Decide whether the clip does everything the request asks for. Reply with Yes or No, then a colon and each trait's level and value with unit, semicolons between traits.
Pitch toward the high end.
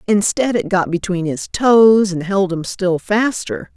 Yes: high, 195 Hz